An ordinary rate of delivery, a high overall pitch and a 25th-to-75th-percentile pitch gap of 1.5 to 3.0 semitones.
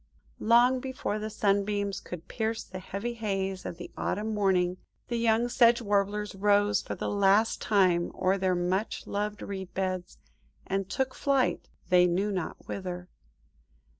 Yes: average, 150 wpm; high, 200 Hz; average, 2.7 semitones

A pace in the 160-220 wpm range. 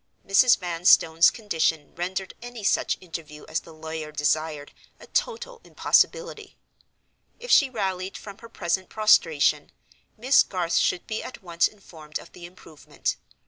No: average, 140 wpm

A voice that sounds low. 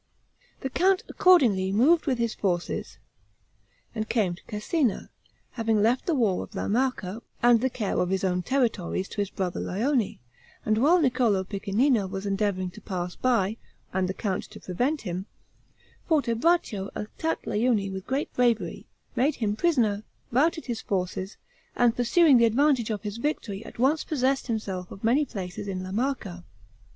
No: high, 220 Hz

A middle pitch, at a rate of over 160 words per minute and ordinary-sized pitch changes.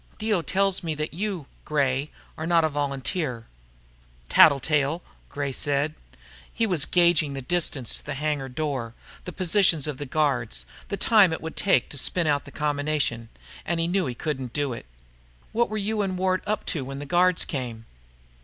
Yes: medium, 150 Hz; average, 180 wpm; average, 4.6 semitones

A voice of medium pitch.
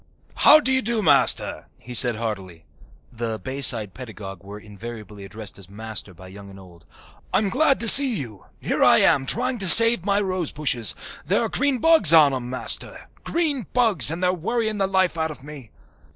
Yes: medium, 145 Hz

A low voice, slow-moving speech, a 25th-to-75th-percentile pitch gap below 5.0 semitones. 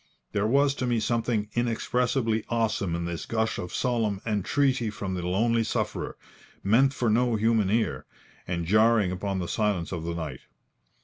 No: low, 110 Hz; average, 165 wpm; average, 3.9 semitones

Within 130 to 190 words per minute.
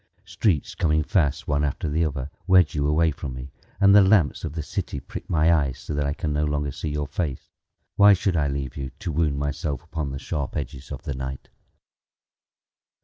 No: fast, 205 wpm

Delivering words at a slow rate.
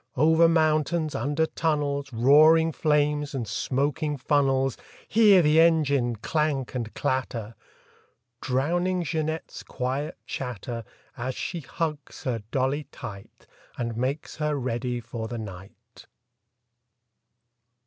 Yes: slow, 105 wpm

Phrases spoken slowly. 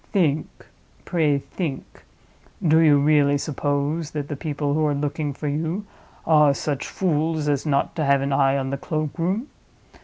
No: average, 160 wpm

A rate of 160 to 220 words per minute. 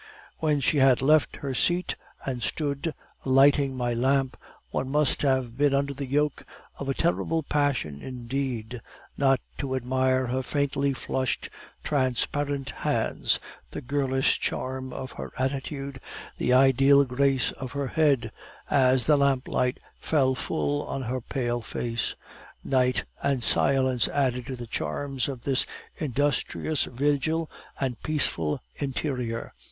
No: slow, 135 wpm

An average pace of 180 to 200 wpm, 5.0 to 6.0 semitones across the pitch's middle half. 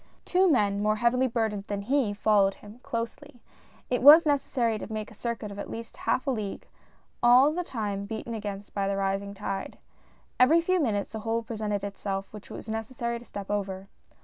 No: average, 195 wpm; average, 3.4 semitones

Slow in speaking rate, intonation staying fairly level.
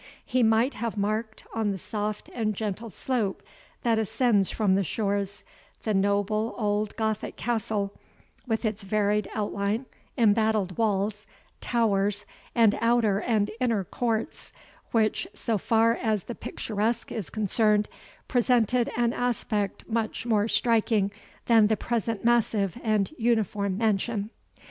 Yes: slow, 130 wpm; narrow, 2.1 semitones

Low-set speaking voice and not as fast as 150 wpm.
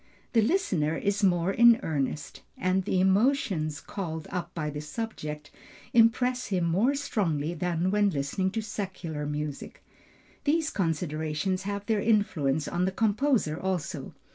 No: medium, 185 Hz; average, 140 wpm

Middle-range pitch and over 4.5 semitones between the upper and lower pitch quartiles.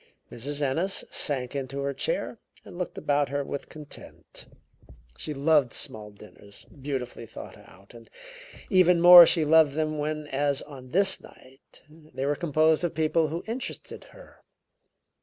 No: medium, 145 Hz; average, 3.1 semitones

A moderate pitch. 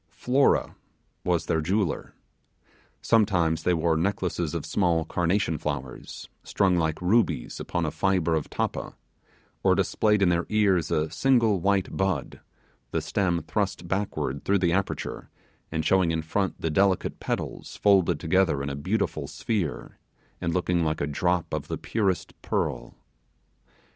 No: very low, 90 Hz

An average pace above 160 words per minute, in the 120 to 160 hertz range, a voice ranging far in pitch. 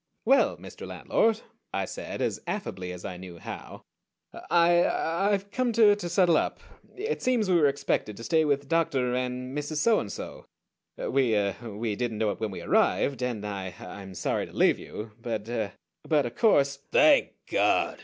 Yes: average, 180 wpm; low, 135 Hz; wide, 8.4 semitones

